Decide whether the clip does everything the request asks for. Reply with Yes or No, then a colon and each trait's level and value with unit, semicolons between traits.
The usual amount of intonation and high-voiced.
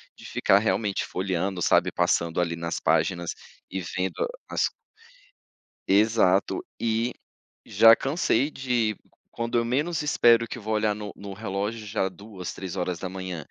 No: average, 3.7 semitones; low, 100 Hz